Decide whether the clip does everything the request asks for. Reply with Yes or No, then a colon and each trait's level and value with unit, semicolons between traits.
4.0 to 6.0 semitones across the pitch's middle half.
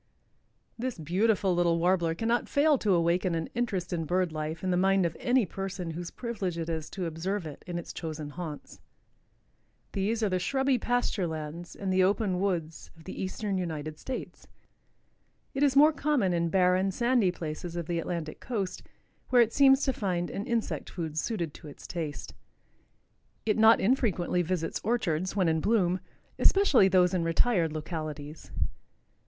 Yes: average, 4.8 semitones